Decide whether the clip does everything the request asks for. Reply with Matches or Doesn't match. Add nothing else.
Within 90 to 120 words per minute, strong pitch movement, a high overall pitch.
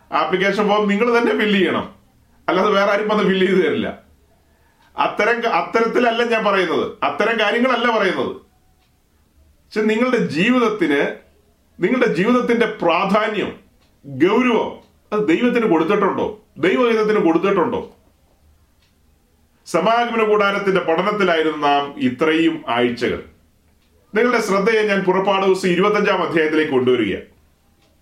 Matches